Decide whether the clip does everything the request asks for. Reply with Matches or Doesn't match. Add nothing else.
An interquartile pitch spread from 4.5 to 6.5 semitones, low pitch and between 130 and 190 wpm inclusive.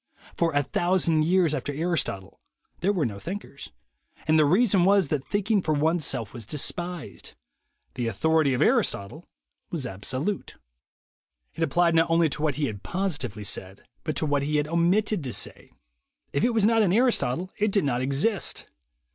Doesn't match